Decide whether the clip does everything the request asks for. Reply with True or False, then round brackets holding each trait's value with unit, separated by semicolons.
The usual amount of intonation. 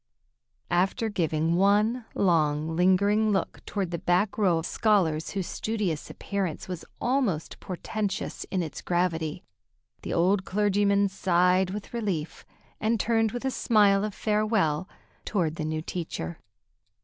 True (3.8 semitones)